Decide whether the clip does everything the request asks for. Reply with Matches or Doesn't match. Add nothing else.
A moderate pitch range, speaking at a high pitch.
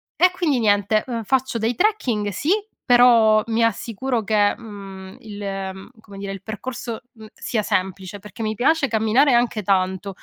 Matches